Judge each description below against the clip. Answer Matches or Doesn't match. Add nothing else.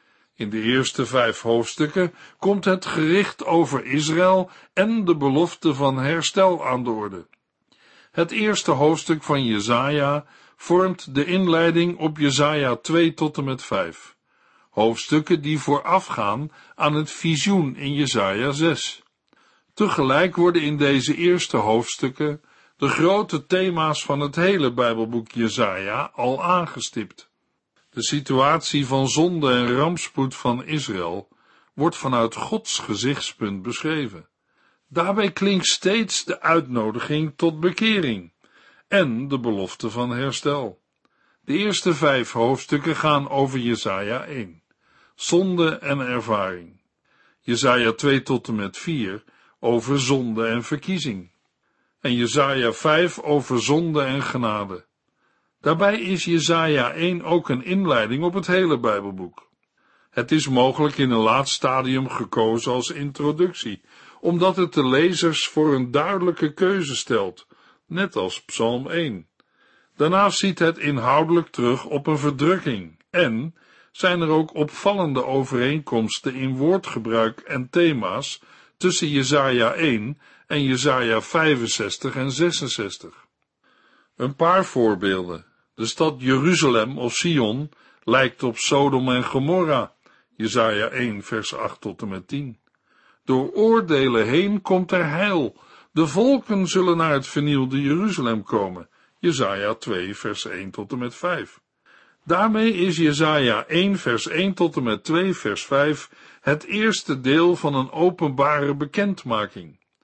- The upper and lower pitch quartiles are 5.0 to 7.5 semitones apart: Matches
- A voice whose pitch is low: Doesn't match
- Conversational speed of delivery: Doesn't match